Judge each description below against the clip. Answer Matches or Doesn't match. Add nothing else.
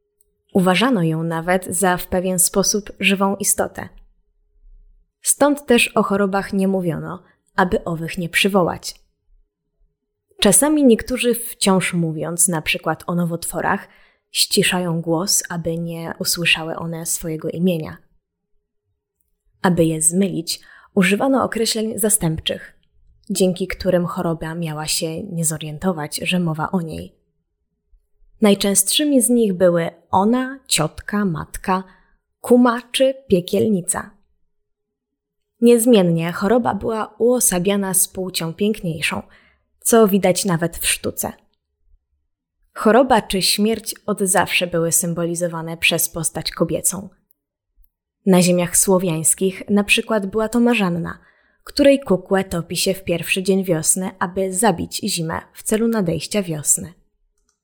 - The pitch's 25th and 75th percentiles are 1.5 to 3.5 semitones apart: Doesn't match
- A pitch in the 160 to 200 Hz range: Matches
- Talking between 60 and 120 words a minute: Matches